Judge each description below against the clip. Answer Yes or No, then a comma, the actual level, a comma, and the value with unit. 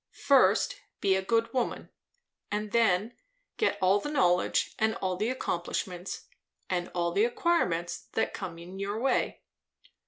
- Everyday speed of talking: Yes, average, 145 wpm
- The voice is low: No, high, 195 Hz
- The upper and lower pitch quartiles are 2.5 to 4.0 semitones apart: No, average, 4.4 semitones